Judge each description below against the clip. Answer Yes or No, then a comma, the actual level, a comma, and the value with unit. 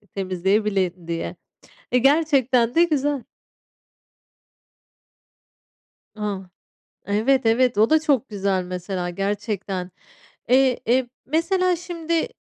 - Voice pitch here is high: Yes, high, 230 Hz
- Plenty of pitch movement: Yes, wide, 6.5 semitones